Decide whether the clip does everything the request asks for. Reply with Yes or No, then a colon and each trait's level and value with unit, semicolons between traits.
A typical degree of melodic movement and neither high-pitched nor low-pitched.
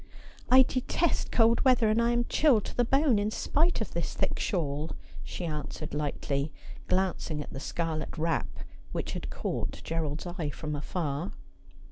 No: wide, 7.5 semitones; medium, 175 Hz